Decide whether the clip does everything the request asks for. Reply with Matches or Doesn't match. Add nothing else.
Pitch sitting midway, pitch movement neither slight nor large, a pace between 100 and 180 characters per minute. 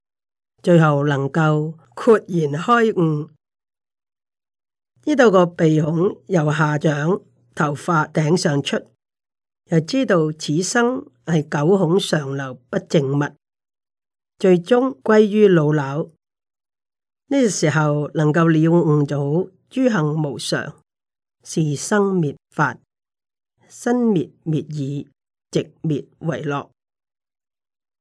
Matches